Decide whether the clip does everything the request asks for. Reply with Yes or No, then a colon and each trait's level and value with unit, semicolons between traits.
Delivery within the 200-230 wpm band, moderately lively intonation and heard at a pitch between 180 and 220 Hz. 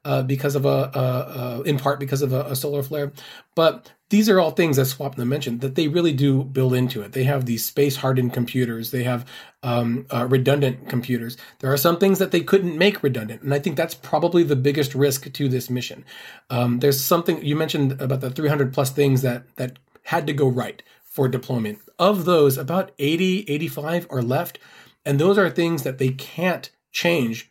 No: fast, 205 wpm; average, 3.9 semitones; medium, 140 Hz